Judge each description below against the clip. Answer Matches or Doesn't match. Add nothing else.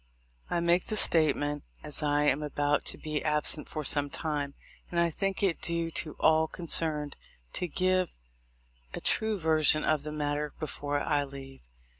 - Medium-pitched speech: Matches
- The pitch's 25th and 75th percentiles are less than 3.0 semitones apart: Matches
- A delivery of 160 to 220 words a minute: Matches